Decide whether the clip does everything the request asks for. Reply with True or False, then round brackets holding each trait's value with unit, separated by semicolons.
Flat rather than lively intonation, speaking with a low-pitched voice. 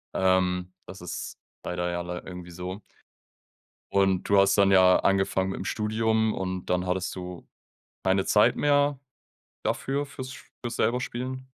False (3.6 semitones; 95 Hz)